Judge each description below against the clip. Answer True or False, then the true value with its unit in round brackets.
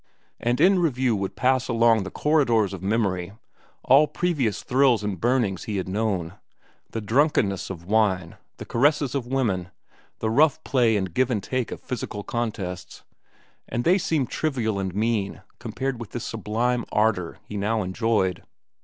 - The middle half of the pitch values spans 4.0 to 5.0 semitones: True (4.7 semitones)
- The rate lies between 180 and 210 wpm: False (155 wpm)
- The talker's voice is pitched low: True (115 Hz)